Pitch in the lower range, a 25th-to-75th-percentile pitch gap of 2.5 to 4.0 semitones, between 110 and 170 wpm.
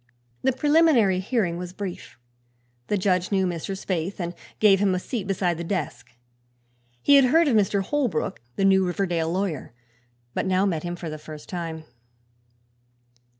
No: medium, 185 Hz; average, 3.0 semitones; average, 160 wpm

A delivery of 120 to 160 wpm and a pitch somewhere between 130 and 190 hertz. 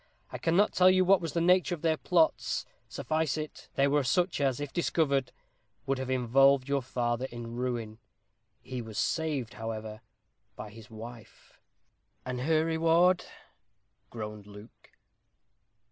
Yes: average, 145 wpm; low, 135 Hz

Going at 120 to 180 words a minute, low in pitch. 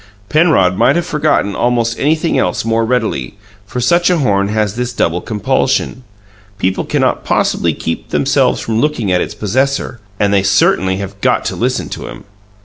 Yes: average, 170 wpm; low, 115 Hz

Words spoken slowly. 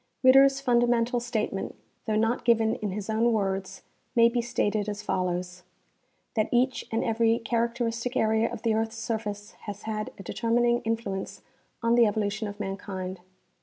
No: average, 155 wpm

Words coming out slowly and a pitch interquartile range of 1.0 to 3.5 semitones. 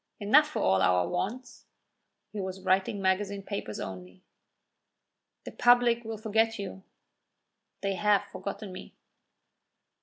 Yes: slow, 120 wpm; average, 3.0 semitones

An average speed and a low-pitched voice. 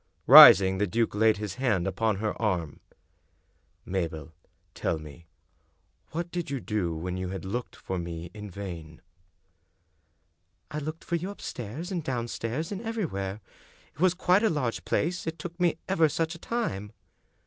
Yes: average, 170 wpm; low, 110 Hz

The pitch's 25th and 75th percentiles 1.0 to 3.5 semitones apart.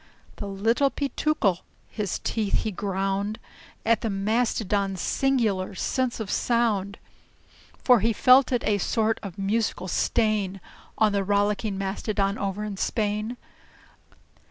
Yes: average, 2.7 semitones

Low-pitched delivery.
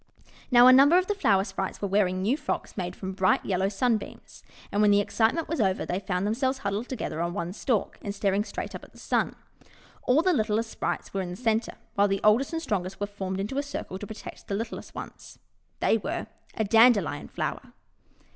No: high, 210 Hz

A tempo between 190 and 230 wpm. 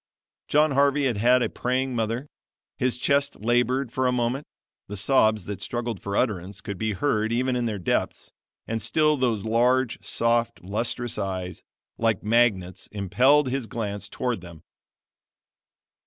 No: average, 150 wpm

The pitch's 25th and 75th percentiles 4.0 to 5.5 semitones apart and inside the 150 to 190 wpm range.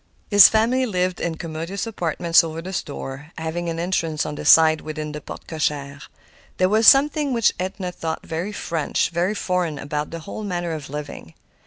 No: average, 3.3 semitones; average, 180 wpm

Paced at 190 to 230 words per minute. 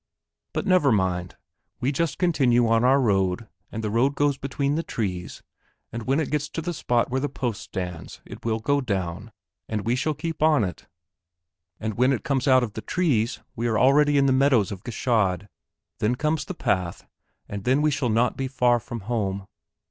Yes: average, 200 wpm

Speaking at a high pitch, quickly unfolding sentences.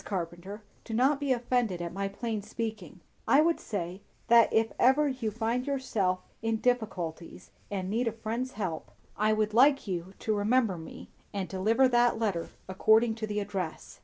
No: high, 215 Hz; average, 170 wpm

